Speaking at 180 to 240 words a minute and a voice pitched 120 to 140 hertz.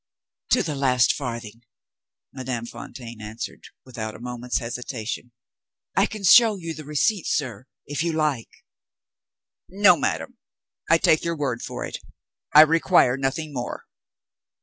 No: slow, 135 wpm; low, 135 Hz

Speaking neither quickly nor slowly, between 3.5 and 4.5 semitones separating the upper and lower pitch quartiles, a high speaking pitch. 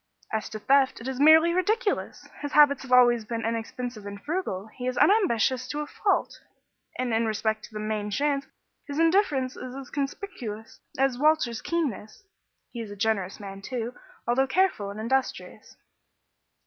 No: average, 165 wpm; average, 4.9 semitones; very high, 255 Hz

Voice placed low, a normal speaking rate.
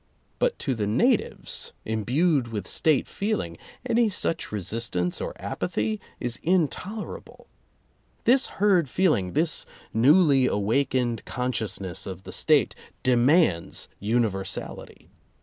No: low, 125 Hz; slow, 110 wpm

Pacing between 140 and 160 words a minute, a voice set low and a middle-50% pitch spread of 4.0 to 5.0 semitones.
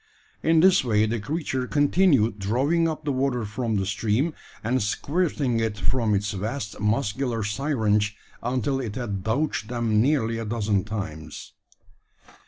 Yes: average, 145 wpm; low, 115 Hz; average, 4.6 semitones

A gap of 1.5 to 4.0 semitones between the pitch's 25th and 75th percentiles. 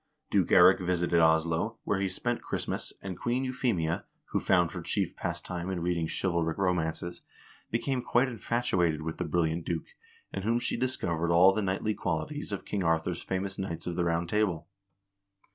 Yes: average, 3.6 semitones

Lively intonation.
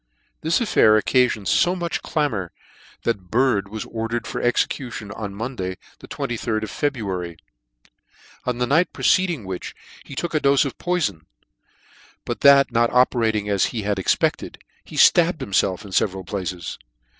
Yes: wide, 5.7 semitones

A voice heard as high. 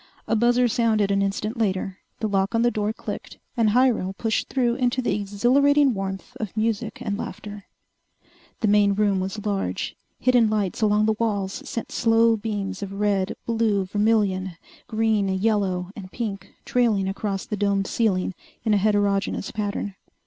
Yes: high, 210 Hz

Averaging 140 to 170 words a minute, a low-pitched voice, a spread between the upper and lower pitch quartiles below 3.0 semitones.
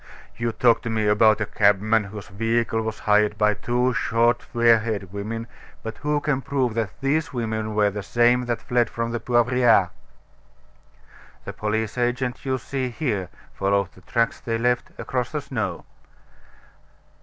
Yes: average, 160 wpm; low, 115 Hz; narrow, 2.6 semitones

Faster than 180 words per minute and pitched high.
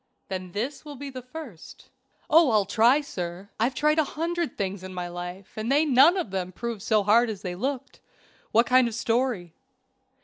Yes: average, 195 wpm; high, 230 Hz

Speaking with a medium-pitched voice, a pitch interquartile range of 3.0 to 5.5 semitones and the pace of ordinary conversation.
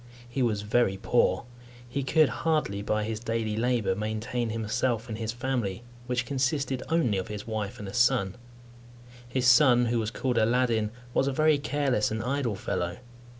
No: low, 120 Hz; average, 3.3 semitones; average, 170 wpm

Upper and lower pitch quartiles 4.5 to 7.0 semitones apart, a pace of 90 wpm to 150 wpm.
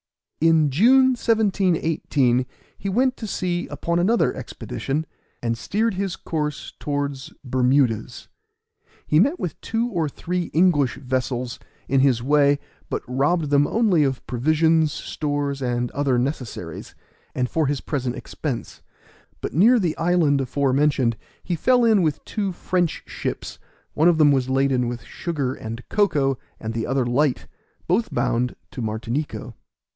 Yes: average, 5.3 semitones; average, 140 wpm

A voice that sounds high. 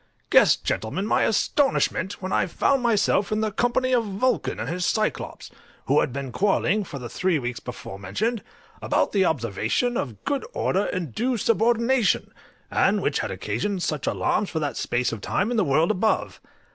Yes: high, 195 Hz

